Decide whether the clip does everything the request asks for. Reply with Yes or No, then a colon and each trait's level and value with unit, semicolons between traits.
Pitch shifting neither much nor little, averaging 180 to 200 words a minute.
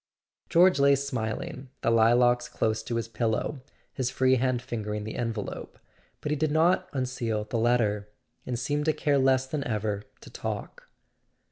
No: average, 3.7 semitones; average, 160 wpm